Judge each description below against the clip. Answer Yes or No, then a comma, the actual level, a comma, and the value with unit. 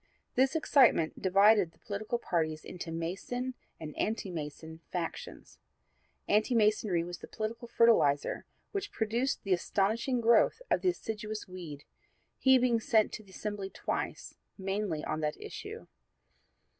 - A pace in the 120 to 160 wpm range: Yes, slow, 135 wpm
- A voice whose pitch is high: Yes, high, 210 Hz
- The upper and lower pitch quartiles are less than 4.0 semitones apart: No, average, 5.2 semitones